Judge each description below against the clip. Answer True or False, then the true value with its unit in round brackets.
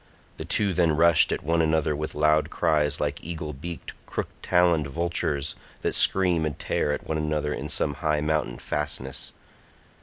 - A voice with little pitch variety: True (2.0 semitones)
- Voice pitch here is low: True (75 Hz)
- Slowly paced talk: False (170 wpm)